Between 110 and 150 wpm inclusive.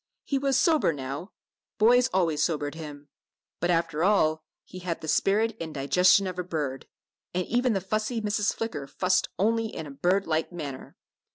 No: average, 175 wpm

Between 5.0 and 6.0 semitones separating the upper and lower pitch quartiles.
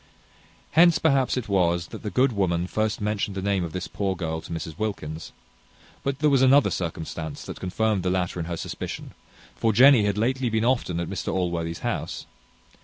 Yes: wide, 5.5 semitones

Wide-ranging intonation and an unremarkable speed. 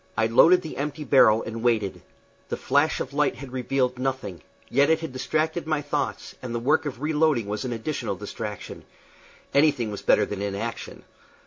No: average, 4.9 semitones; average, 180 wpm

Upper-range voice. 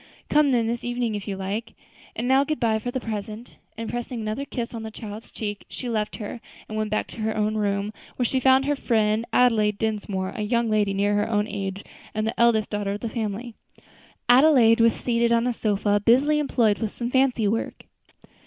Yes: high, 225 Hz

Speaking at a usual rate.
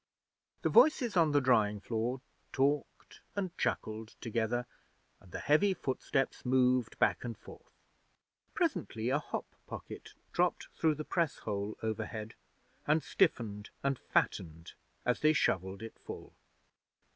No: slow, 130 wpm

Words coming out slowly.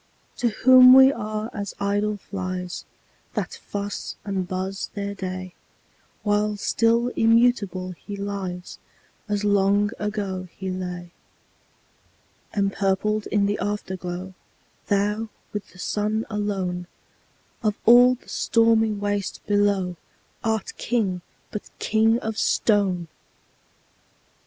Yes: slow, 110 wpm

